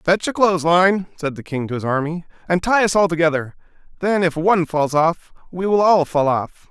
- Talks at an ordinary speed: No, fast, 215 wpm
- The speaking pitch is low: No, medium, 170 Hz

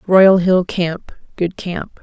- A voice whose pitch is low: No, medium, 180 Hz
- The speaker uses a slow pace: Yes, slow, 120 wpm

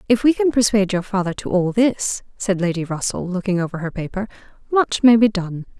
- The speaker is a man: No, female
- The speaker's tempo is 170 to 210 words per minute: Yes, fast, 205 wpm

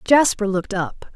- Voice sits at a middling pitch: No, high, 210 Hz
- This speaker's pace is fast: No, average, 155 wpm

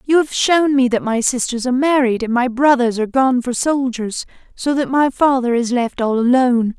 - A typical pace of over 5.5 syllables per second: No, 5.2 syllables/s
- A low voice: No, very high, 255 Hz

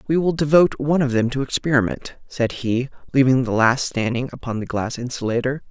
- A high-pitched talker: No, low, 130 Hz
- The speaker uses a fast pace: No, average, 190 wpm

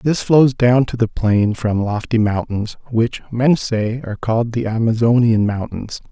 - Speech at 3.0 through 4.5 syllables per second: Yes, 4.4 syllables/s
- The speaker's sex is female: No, male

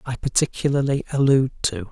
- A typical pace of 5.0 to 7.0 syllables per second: Yes, 5.9 syllables/s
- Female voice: No, male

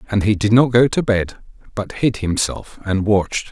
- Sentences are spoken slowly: No, fast, 205 wpm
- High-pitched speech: No, low, 105 Hz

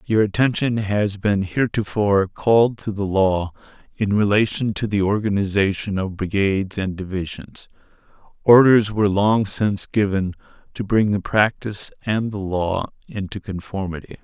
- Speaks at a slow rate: Yes, slow, 130 wpm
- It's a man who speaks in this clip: Yes, male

